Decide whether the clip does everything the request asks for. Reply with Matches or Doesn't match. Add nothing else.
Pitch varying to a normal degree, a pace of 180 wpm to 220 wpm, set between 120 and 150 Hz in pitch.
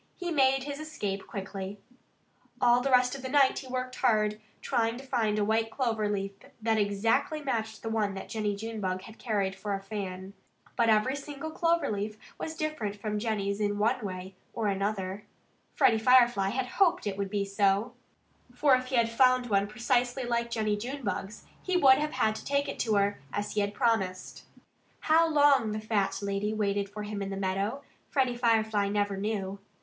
Doesn't match